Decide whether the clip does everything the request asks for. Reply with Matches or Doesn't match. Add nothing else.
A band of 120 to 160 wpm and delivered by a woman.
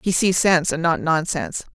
Doesn't match